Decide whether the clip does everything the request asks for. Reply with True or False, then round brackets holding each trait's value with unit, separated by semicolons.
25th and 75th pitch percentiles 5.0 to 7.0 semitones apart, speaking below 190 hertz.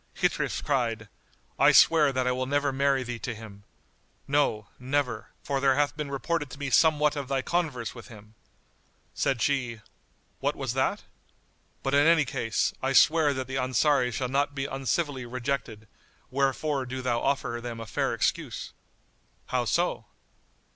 False (2.8 semitones; 135 Hz)